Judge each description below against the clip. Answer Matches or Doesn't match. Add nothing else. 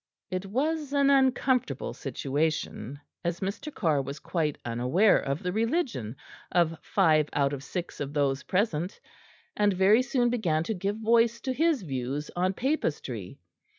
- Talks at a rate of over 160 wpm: Doesn't match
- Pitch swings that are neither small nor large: Doesn't match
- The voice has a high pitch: Doesn't match